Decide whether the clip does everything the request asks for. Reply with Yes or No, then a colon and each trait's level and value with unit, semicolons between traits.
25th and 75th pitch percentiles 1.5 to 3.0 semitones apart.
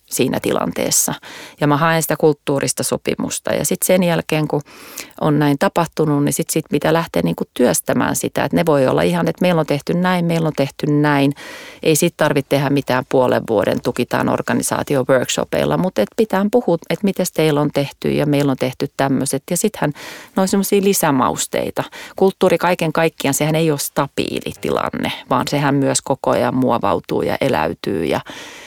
No: average, 3.8 semitones